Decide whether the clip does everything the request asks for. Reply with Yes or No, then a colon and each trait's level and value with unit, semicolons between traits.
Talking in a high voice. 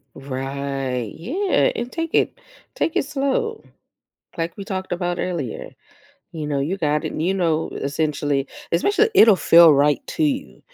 No: medium, 170 Hz